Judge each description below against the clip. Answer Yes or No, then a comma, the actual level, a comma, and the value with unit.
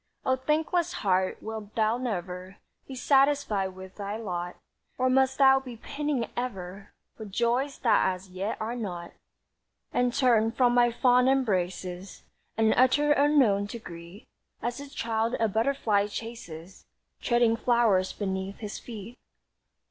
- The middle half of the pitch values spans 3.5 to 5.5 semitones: Yes, average, 4.7 semitones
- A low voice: No, high, 225 Hz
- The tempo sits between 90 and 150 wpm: Yes, average, 140 wpm